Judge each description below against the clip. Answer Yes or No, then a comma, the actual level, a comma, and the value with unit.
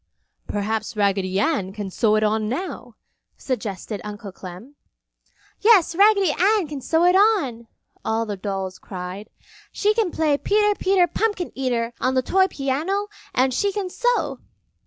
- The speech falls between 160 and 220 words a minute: No, average, 150 wpm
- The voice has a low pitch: No, very high, 265 Hz